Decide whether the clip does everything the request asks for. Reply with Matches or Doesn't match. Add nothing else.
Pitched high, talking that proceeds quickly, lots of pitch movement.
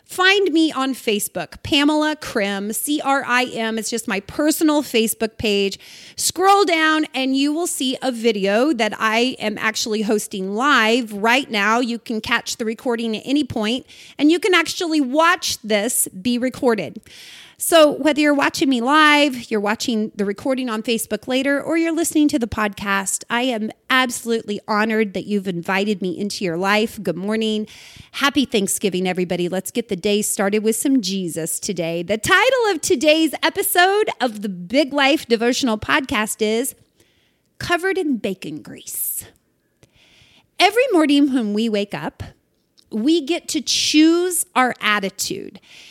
Doesn't match